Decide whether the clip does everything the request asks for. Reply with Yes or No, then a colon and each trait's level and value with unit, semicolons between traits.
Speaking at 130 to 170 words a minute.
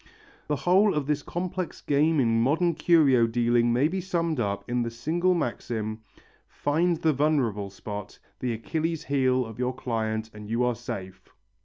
Yes: average, 165 wpm